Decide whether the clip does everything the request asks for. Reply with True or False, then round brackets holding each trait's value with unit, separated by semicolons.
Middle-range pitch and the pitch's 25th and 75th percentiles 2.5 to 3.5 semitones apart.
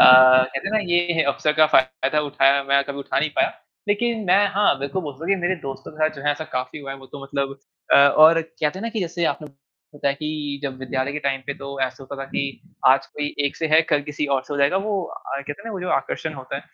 True (145 Hz; 2.9 semitones)